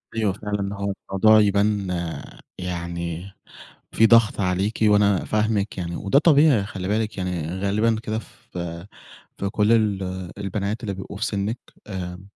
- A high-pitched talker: No, low, 100 Hz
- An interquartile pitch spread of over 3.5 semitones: No, narrow, 2.5 semitones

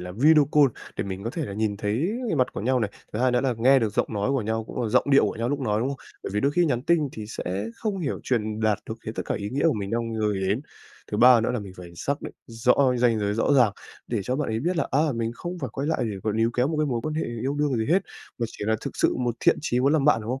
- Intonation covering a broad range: No, average, 4.3 semitones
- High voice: No, low, 120 Hz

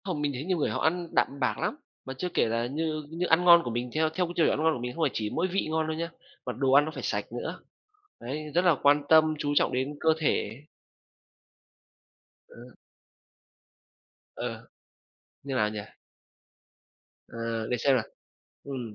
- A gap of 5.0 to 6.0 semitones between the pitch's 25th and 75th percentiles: No, average, 4.4 semitones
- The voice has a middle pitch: Yes, medium, 150 Hz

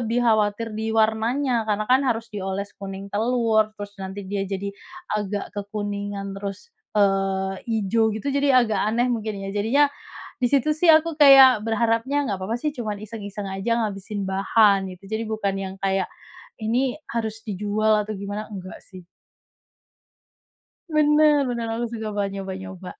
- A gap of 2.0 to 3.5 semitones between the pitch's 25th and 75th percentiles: Yes, average, 2.9 semitones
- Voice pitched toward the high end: Yes, high, 215 Hz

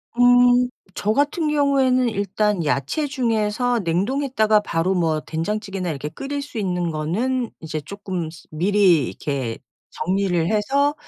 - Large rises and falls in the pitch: Yes, wide, 6.7 semitones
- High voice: Yes, high, 210 Hz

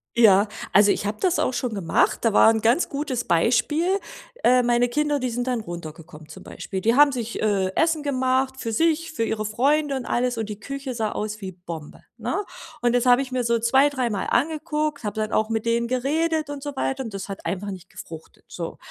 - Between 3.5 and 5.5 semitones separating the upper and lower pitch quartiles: Yes, average, 4.7 semitones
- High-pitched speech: Yes, high, 240 Hz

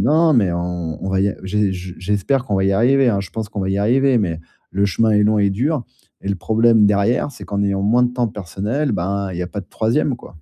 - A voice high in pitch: No, low, 105 Hz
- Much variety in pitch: No, average, 3.7 semitones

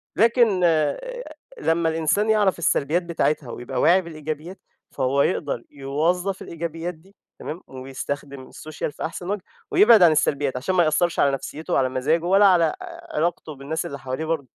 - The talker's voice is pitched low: No, medium, 160 Hz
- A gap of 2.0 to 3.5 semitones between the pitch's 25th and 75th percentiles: No, average, 4.3 semitones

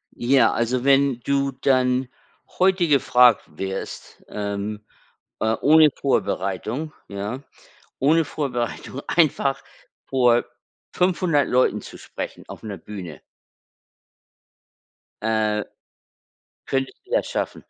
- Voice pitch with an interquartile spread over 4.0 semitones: Yes, average, 4.5 semitones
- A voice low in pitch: Yes, low, 130 Hz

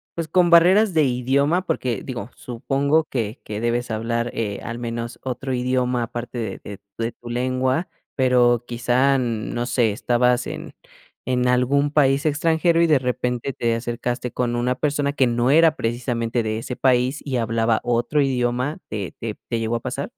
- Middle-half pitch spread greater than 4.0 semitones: No, average, 2.7 semitones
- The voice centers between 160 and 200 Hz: No, low, 125 Hz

